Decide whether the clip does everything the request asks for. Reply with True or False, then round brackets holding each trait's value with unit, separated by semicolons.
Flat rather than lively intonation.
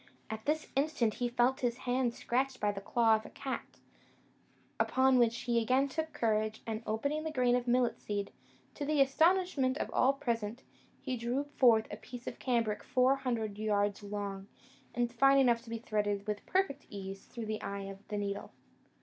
False (3.7 semitones)